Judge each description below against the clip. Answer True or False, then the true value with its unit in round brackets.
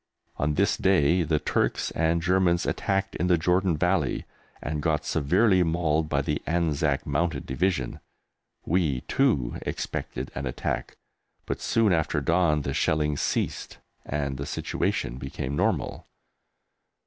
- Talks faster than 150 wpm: False (135 wpm)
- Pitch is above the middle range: False (80 Hz)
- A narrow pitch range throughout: False (3.9 semitones)